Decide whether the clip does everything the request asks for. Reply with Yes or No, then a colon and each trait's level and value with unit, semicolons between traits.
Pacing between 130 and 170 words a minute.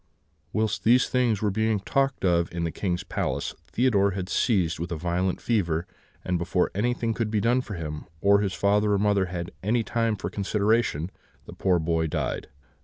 No: average, 185 wpm